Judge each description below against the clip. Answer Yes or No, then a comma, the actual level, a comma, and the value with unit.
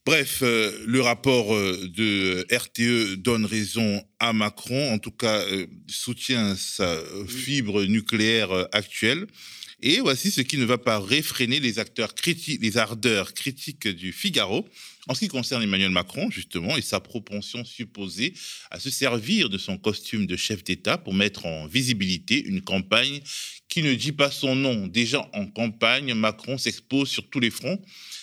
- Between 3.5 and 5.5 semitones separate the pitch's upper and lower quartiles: Yes, average, 4.3 semitones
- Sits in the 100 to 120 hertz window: Yes, low, 115 Hz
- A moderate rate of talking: Yes, average, 160 wpm